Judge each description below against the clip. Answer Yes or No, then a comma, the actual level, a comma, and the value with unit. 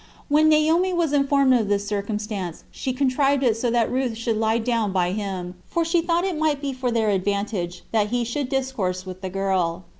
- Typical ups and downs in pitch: No, wide, 5.7 semitones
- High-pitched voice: Yes, high, 230 Hz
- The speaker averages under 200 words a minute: No, fast, 205 wpm